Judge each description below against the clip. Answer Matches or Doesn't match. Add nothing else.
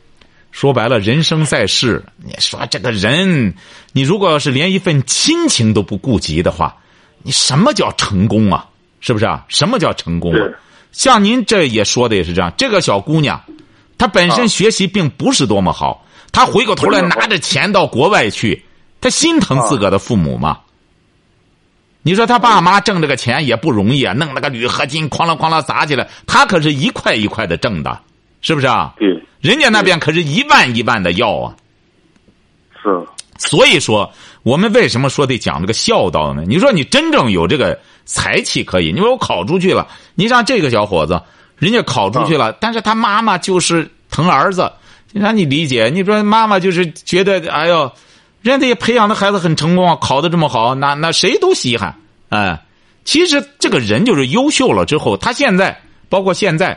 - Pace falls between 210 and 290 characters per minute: Matches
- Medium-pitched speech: Matches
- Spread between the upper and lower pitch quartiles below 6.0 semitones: Doesn't match